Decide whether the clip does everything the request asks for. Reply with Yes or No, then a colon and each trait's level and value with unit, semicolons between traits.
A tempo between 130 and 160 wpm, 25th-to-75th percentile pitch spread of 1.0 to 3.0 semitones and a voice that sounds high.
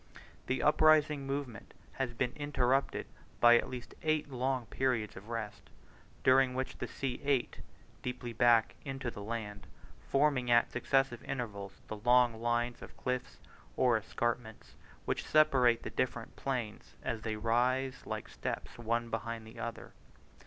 No: average, 145 wpm; narrow, 2.5 semitones; low, 120 Hz